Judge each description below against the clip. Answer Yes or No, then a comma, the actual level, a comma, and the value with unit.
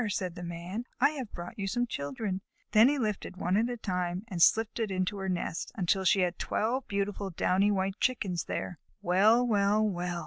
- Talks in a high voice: Yes, high, 195 Hz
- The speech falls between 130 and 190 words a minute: No, average, 200 wpm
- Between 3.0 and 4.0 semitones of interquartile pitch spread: Yes, average, 3.3 semitones